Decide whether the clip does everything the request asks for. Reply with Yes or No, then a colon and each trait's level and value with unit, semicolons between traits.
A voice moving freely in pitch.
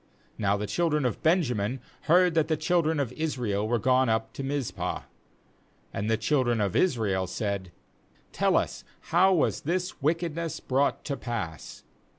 Yes: wide, 6.7 semitones